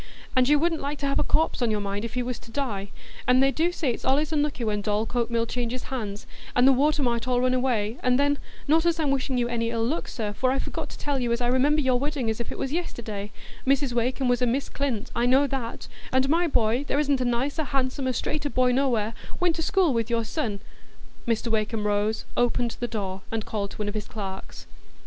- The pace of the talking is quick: Yes, fast, 245 wpm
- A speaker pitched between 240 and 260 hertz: Yes, very high, 250 Hz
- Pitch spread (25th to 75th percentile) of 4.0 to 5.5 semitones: No, average, 3.6 semitones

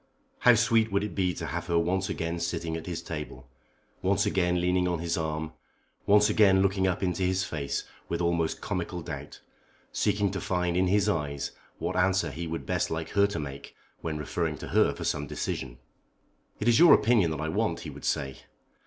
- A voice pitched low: Yes, very low, 90 Hz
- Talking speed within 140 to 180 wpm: No, average, 200 wpm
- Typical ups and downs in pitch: Yes, average, 3.2 semitones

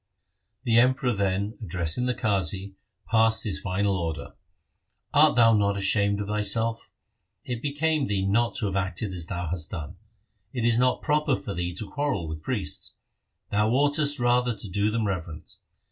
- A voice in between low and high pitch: No, low, 105 Hz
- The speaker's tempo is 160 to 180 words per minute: Yes, average, 170 wpm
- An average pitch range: Yes, average, 4.3 semitones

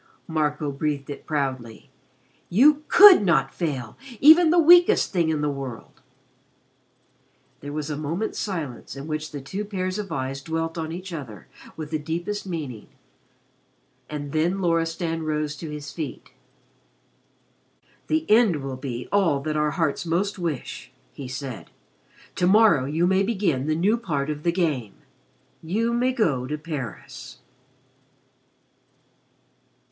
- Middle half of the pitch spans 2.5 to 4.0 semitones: No, average, 4.8 semitones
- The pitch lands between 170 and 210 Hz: No, medium, 160 Hz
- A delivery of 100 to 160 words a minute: Yes, average, 140 wpm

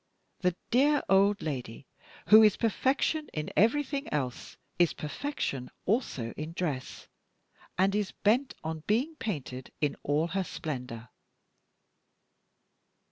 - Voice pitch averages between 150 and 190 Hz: Yes, medium, 185 Hz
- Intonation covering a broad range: Yes, wide, 7.8 semitones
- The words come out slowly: Yes, slow, 115 wpm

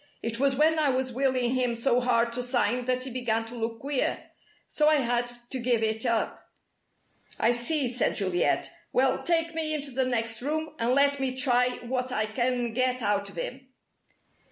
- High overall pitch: Yes, very high, 250 Hz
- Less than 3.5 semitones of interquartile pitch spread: Yes, narrow, 2.4 semitones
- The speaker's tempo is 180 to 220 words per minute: Yes, average, 190 wpm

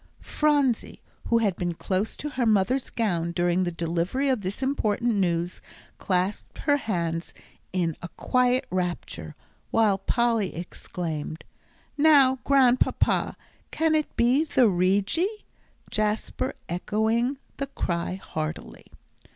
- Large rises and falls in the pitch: Yes, wide, 6.6 semitones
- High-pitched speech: Yes, high, 210 Hz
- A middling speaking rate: No, slow, 120 wpm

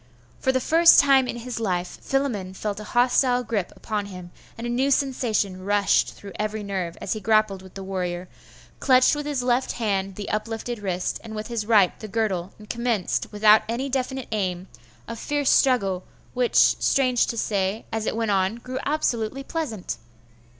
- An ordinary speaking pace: Yes, average, 185 wpm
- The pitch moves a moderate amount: Yes, average, 4.3 semitones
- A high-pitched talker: Yes, high, 220 Hz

